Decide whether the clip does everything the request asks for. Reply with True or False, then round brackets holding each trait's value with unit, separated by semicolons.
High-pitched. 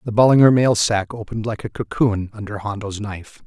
False (110 Hz)